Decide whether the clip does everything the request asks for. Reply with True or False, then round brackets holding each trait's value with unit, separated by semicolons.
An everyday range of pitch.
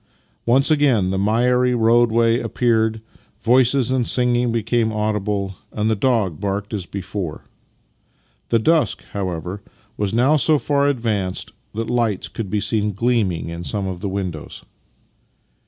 True (3.7 semitones)